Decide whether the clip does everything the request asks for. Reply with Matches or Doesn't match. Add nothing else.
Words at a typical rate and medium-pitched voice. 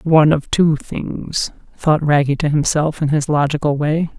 Matches